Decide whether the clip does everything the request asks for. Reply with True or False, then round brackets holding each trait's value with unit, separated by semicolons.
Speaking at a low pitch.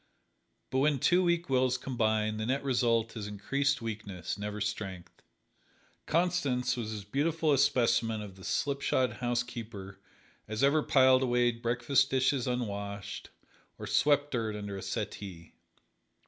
True (120 Hz)